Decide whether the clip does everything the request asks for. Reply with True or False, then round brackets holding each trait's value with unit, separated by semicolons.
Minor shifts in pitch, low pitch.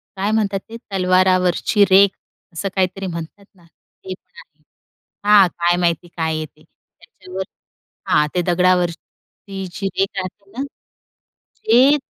False (2.2 semitones; 185 Hz)